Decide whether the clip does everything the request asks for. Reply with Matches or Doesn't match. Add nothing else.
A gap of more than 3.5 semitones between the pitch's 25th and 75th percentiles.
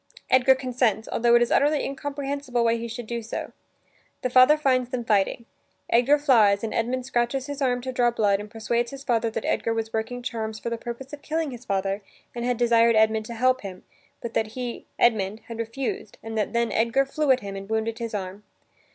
Doesn't match